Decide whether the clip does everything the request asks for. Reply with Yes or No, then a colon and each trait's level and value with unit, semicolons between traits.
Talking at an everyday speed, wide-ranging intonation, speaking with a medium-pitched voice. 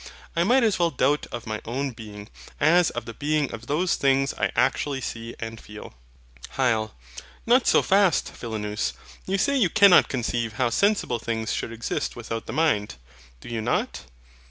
No: average, 175 wpm; wide, 7.0 semitones; low, 125 Hz